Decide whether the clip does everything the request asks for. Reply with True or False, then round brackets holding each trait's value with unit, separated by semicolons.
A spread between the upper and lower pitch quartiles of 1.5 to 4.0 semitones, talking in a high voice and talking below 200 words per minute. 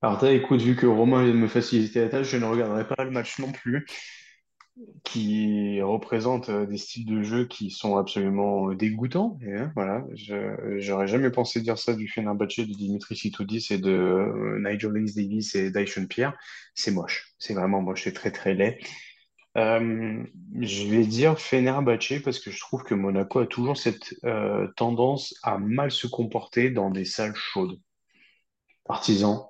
False (3.3 semitones; 115 Hz; 175 wpm)